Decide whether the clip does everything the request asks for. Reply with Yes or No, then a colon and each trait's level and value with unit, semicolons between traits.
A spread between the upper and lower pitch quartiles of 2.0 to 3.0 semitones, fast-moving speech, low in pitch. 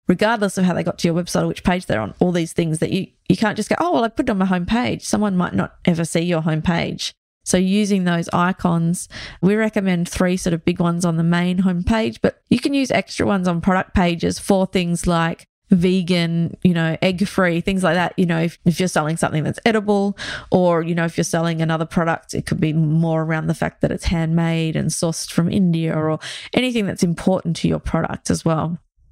No: narrow, 2.4 semitones; fast, 230 wpm; medium, 175 Hz